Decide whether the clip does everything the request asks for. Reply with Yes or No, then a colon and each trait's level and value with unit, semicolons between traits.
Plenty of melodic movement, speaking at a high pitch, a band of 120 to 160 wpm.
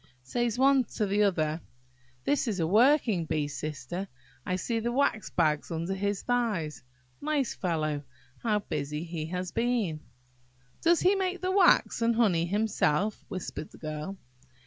Yes: wide, 6.9 semitones; high, 195 Hz; average, 155 wpm